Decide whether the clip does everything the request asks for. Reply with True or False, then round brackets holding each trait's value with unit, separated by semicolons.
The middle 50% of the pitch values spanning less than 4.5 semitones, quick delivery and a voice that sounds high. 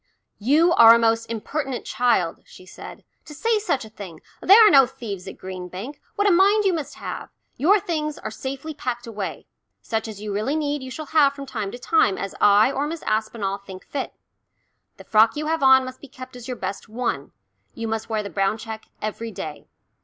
False (5.6 semitones; 215 wpm; 240 Hz)